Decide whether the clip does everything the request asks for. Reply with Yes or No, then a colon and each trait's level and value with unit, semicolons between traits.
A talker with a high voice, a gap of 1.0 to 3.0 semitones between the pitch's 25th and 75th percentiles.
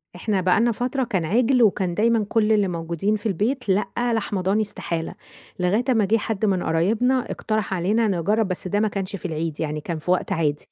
No: high, 200 Hz; average, 3.8 semitones